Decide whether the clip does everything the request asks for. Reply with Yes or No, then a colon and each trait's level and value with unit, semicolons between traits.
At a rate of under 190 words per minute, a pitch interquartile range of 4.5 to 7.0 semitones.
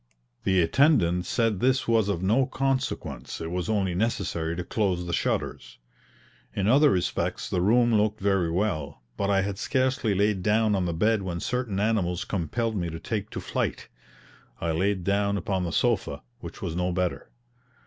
No: average, 175 wpm; average, 4.0 semitones